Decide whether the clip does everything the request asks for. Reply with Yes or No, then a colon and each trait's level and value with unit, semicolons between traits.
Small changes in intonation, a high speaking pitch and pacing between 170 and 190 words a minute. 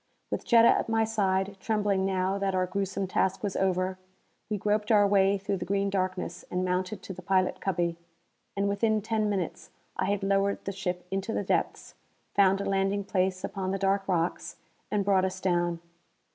Yes: narrow, 1.3 semitones; high, 195 Hz; average, 185 wpm